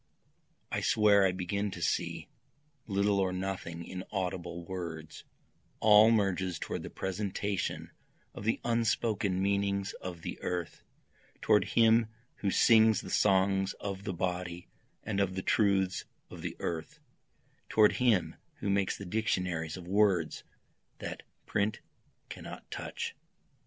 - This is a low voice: Yes, very low, 95 Hz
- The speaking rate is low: Yes, slow, 130 wpm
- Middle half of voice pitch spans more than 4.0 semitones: No, narrow, 2.4 semitones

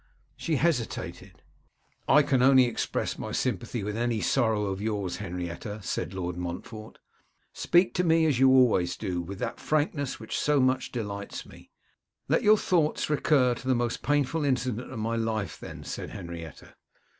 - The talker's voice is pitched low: Yes, low, 120 Hz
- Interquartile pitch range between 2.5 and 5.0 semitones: No, wide, 5.4 semitones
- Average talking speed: Yes, average, 165 wpm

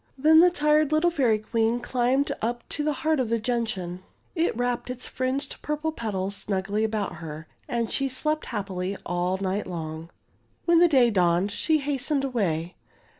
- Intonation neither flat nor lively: No, wide, 7.1 semitones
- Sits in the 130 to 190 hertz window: No, high, 235 Hz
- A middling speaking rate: Yes, average, 170 wpm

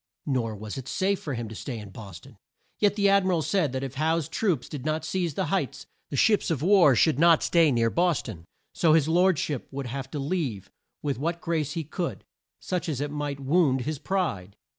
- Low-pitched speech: No, medium, 150 Hz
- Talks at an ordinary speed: No, fast, 225 wpm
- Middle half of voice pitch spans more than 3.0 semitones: Yes, average, 4.8 semitones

